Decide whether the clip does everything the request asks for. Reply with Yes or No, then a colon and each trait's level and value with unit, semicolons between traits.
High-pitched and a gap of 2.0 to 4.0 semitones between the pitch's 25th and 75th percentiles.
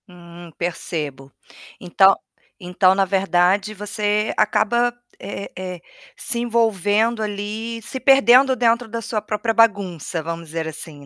No: high, 205 Hz; average, 4.4 semitones